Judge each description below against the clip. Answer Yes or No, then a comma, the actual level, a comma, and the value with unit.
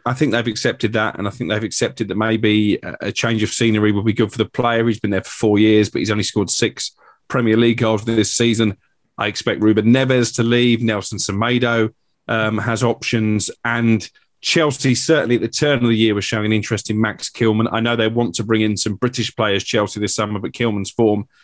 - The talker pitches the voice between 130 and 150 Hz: No, low, 110 Hz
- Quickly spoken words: Yes, fast, 225 wpm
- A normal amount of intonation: No, narrow, 1.7 semitones